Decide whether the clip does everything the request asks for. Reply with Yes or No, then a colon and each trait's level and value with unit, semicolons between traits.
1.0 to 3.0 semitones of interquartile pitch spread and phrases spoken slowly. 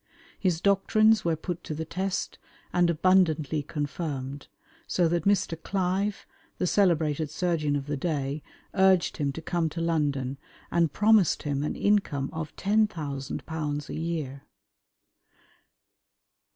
No: average, 4.0 semitones; slow, 125 wpm